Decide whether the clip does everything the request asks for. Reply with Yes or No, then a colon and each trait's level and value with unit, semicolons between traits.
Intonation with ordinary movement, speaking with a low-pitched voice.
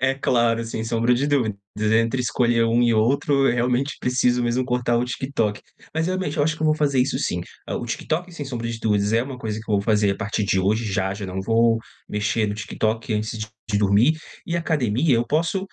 Yes: average, 3.8 semitones; low, 120 Hz